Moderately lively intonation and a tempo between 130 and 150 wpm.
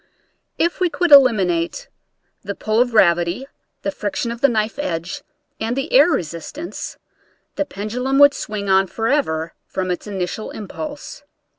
No: wide, 6.8 semitones; average, 145 wpm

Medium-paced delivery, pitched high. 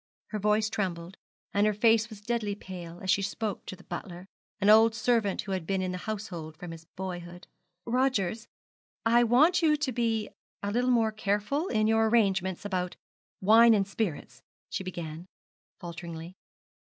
Yes: average, 170 wpm; high, 205 Hz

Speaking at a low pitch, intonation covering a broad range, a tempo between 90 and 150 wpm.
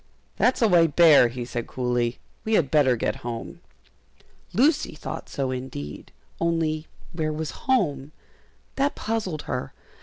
No: medium, 155 Hz; wide, 5.9 semitones; average, 140 wpm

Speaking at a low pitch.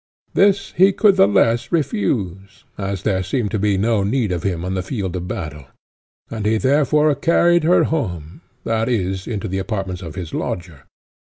Yes: low, 100 Hz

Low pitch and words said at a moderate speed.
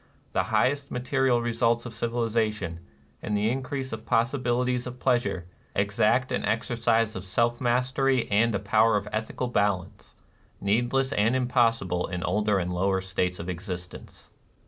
Yes: low, 115 Hz; average, 145 wpm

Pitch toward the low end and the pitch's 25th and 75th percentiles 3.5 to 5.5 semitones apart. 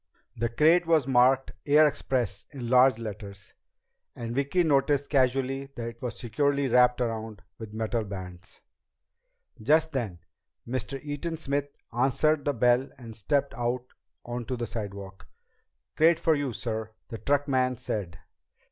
Yes: low, 125 Hz; average, 3.8 semitones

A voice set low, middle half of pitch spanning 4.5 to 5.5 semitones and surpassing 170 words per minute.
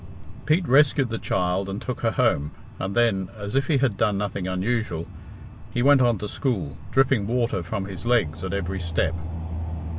Yes: low, 105 Hz; average, 4.9 semitones; average, 180 wpm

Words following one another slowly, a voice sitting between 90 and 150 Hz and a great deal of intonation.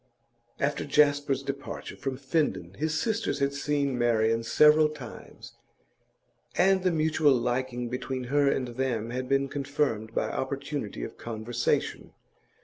No: slow, 130 wpm; low, 135 Hz; average, 3.3 semitones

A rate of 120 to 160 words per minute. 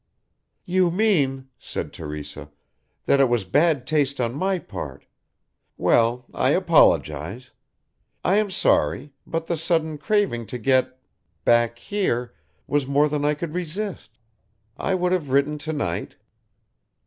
Yes: slow, 135 wpm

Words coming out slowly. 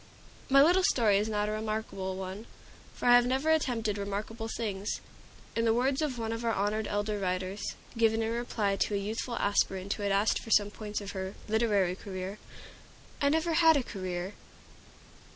No: average, 185 wpm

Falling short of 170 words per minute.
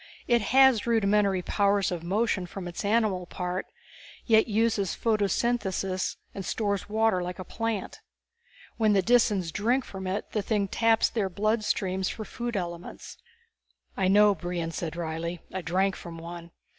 Yes: average, 155 wpm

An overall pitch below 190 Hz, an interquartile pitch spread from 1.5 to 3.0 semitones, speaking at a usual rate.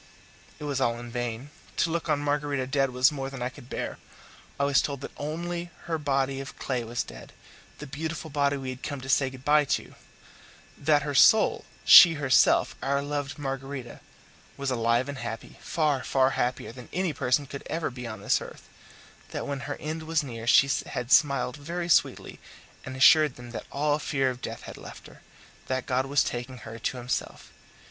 Yes: low, 135 Hz; narrow, 2.6 semitones; average, 195 wpm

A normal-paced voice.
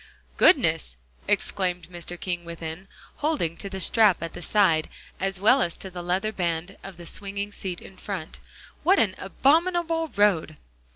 Yes: average, 160 wpm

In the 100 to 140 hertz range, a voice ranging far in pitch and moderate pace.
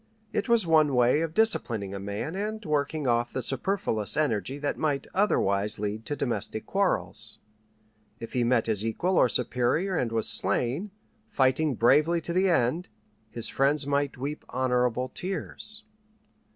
Yes: low, 135 Hz; wide, 5.8 semitones; average, 150 wpm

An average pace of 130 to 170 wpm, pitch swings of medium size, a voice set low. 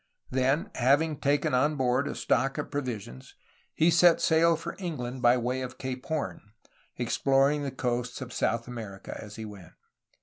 Yes: average, 165 wpm; average, 3.1 semitones; low, 130 Hz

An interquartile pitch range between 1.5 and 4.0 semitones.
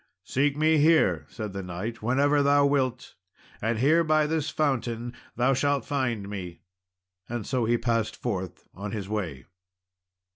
No: average, 5.1 semitones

